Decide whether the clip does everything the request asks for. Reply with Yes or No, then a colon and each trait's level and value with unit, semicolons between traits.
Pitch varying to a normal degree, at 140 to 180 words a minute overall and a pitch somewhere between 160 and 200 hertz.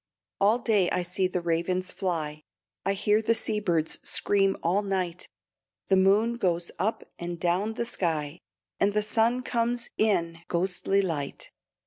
Yes: average, 3.6 semitones; average, 150 wpm; high, 190 Hz